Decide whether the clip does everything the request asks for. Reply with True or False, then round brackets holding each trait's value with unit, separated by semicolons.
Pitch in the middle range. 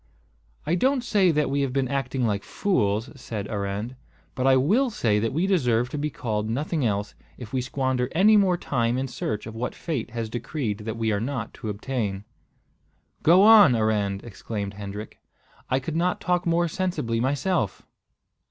False (125 Hz)